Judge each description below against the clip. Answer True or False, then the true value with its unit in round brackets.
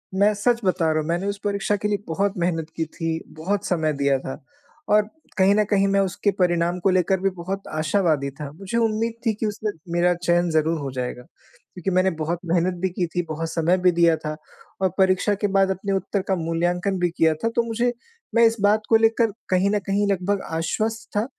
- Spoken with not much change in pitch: False (3.5 semitones)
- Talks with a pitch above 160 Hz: True (185 Hz)